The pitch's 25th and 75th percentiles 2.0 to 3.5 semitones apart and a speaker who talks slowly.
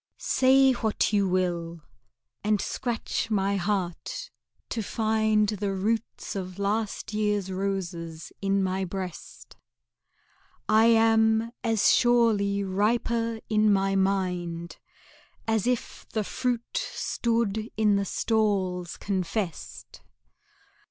Yes: average, 2.7 semitones; slow, 105 wpm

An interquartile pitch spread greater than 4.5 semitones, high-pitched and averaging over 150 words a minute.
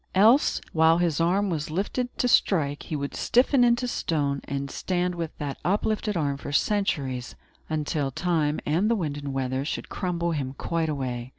No: average, 5.2 semitones; medium, 160 Hz; average, 175 wpm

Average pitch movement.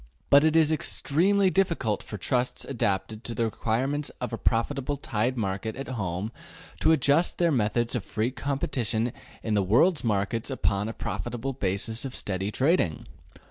Yes: average, 4.9 semitones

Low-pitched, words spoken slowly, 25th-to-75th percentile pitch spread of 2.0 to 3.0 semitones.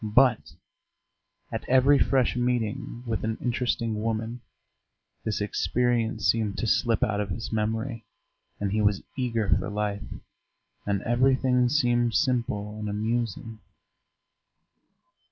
Yes: low, 115 Hz; slow, 120 wpm; narrow, 2.6 semitones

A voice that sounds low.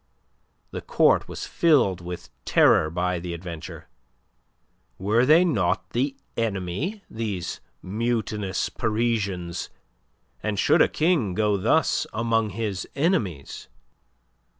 Yes: low, 105 Hz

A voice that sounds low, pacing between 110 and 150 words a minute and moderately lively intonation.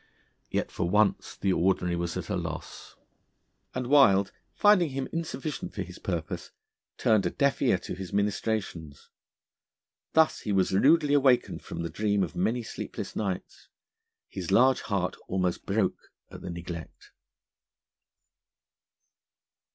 No: low, 100 Hz; slow, 135 wpm; wide, 6.3 semitones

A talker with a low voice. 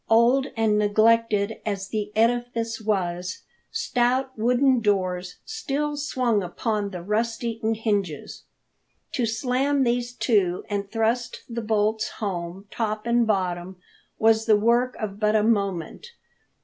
No: high, 220 Hz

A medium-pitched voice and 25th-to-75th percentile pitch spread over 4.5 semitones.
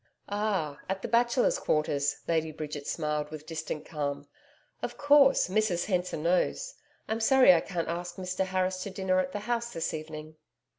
Yes: medium, 180 Hz; average, 4.9 semitones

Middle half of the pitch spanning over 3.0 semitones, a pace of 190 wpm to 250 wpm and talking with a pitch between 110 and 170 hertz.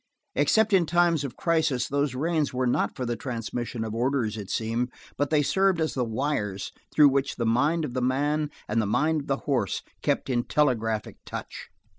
Yes: average, 4.4 semitones; average, 195 wpm; low, 135 Hz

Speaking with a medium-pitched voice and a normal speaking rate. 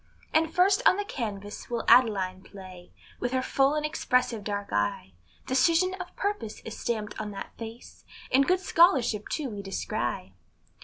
No: high, 235 Hz; average, 160 wpm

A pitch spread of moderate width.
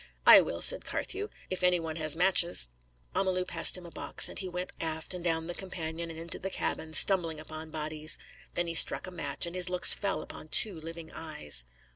No: narrow, 2.3 semitones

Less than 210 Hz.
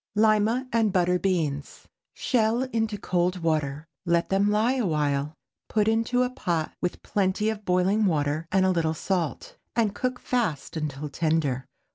Yes: medium, 185 Hz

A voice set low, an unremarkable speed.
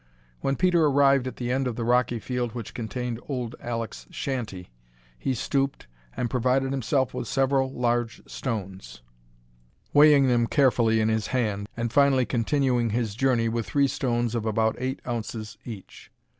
Yes: low, 120 Hz; average, 155 wpm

